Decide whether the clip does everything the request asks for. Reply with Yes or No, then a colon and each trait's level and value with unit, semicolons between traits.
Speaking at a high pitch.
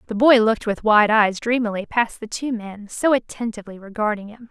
Yes: high, 220 Hz